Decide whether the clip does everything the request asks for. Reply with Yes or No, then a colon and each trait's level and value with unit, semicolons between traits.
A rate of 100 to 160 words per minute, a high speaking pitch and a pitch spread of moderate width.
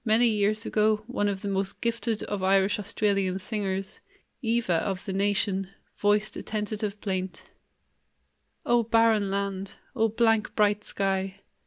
No: average, 140 wpm; high, 205 Hz; narrow, 2.0 semitones